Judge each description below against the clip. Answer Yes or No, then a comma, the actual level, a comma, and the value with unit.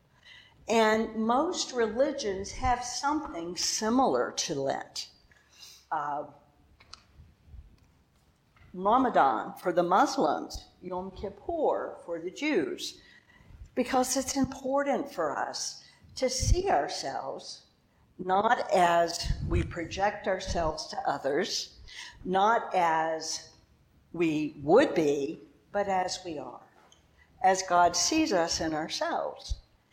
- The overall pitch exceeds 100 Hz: Yes, high, 190 Hz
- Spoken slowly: Yes, slow, 95 wpm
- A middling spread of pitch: No, wide, 8.0 semitones